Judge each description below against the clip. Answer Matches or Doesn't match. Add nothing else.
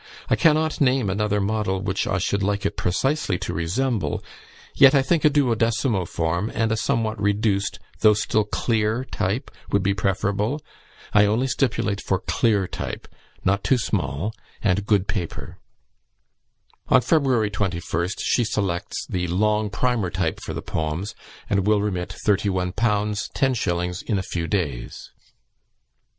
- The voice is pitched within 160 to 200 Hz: Doesn't match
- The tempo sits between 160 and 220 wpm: Doesn't match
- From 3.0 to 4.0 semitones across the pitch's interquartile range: Matches